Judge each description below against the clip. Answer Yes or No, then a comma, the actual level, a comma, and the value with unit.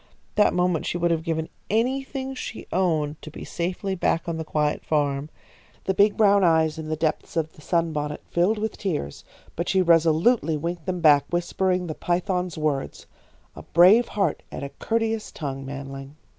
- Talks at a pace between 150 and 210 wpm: Yes, average, 175 wpm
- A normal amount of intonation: Yes, average, 3.7 semitones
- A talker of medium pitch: Yes, medium, 170 Hz